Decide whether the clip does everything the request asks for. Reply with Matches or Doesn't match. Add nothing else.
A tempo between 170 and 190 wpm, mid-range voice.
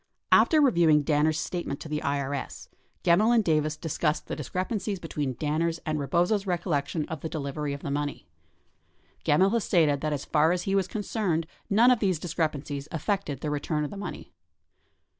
Matches